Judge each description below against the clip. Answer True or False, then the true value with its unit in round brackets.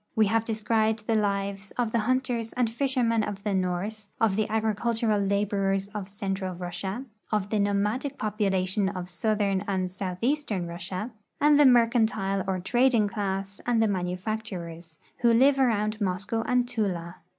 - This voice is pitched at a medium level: False (210 Hz)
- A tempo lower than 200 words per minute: True (155 wpm)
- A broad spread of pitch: False (2.9 semitones)